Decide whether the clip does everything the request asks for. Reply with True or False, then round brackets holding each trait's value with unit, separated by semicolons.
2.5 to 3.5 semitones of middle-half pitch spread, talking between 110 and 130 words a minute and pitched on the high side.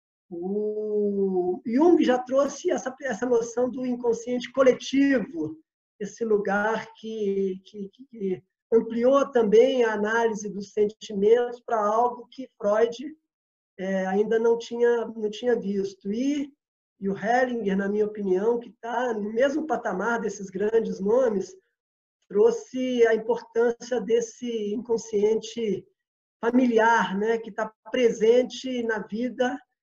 True (2.9 semitones; 120 wpm; 230 Hz)